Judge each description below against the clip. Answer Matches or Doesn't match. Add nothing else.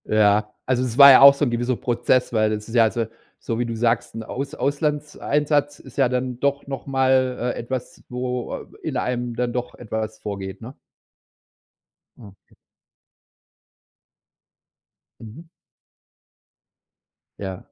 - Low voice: Matches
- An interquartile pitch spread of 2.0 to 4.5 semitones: Matches